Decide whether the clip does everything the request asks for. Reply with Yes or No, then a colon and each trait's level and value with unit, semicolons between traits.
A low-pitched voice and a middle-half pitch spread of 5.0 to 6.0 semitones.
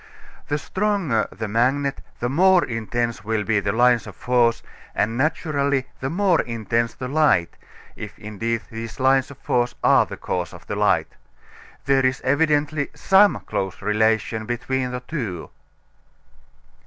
No: low, 125 Hz; average, 4.1 semitones